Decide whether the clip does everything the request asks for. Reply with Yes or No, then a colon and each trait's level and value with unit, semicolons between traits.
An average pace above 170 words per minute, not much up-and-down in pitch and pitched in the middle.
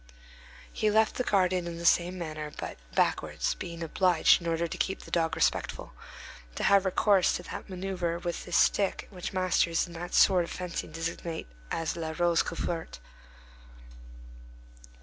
No: average, 160 wpm; narrow, 1.9 semitones; medium, 175 Hz